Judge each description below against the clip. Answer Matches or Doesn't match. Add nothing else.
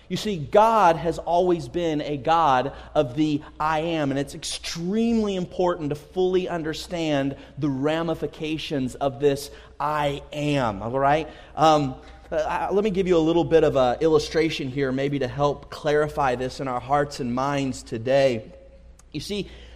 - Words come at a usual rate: Matches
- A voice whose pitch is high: Doesn't match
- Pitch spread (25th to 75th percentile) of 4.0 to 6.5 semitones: Doesn't match